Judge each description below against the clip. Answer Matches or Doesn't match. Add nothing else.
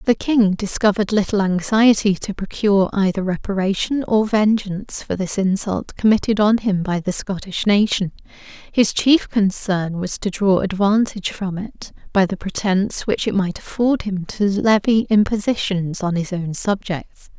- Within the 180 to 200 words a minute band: Doesn't match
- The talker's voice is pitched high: Matches